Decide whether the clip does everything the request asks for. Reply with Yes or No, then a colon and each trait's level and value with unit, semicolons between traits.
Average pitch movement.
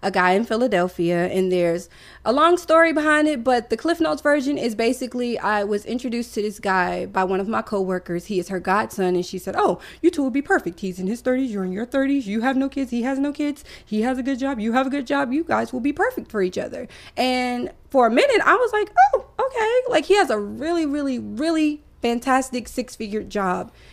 No: wide, 6.2 semitones